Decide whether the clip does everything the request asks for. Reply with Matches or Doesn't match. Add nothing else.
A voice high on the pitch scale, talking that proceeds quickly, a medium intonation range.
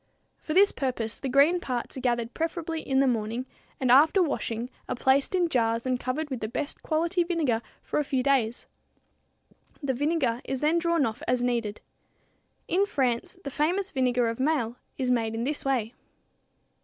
Doesn't match